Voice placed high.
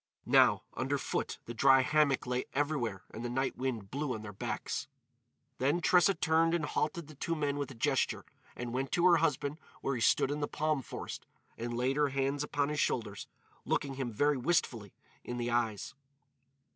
No: low, 135 Hz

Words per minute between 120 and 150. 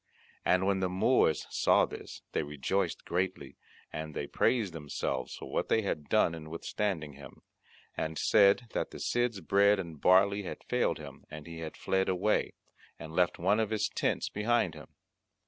No: average, 175 wpm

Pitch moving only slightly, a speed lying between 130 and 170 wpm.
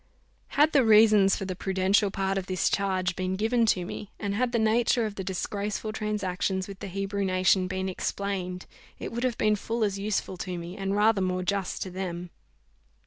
No: narrow, 2.3 semitones; average, 195 wpm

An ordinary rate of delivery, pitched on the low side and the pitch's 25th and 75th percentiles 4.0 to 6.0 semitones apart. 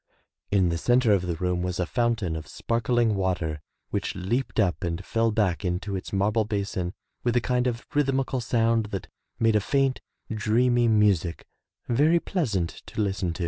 Yes: average, 180 wpm; low, 105 Hz; average, 4.7 semitones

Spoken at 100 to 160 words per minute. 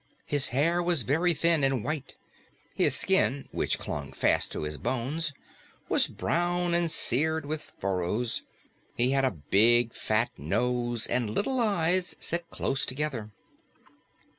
Yes: average, 140 wpm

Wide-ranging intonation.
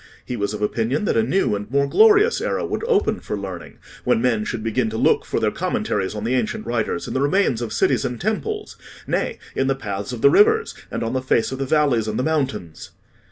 Yes: wide, 6.0 semitones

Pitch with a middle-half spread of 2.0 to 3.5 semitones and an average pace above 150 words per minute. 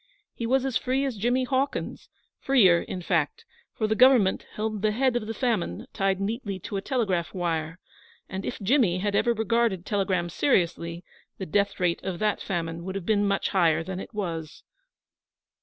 No: average, 4.7 semitones; average, 180 wpm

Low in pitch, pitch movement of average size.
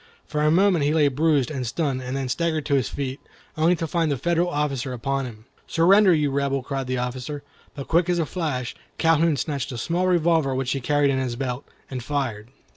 No: medium, 145 Hz; average, 3.8 semitones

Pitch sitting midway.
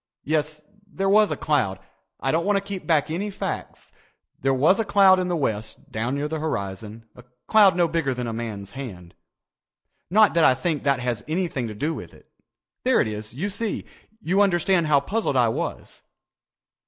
Yes: medium, 155 Hz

